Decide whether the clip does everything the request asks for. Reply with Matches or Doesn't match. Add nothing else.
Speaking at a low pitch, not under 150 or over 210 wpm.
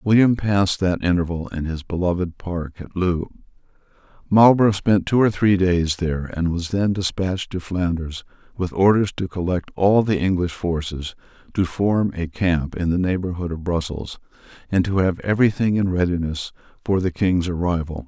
Matches